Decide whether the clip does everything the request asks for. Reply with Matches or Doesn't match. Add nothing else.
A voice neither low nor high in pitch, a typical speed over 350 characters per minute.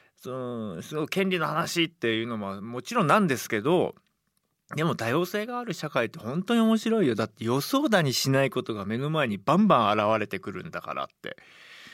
Matches